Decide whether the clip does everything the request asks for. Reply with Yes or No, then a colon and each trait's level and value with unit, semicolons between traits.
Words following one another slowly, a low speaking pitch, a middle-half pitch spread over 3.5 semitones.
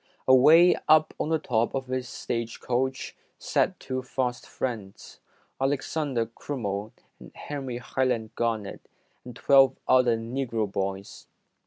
No: slow, 125 wpm; low, 125 Hz; average, 2.8 semitones